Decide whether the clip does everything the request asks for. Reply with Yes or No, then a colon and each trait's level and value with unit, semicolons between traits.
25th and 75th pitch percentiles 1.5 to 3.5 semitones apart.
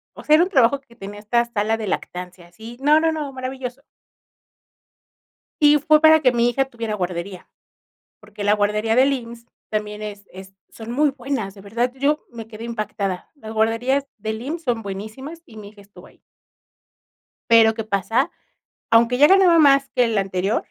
No: average, 4.5 semitones